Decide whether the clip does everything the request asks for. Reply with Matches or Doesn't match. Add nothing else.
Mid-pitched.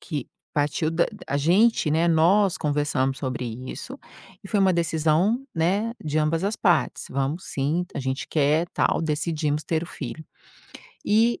Matches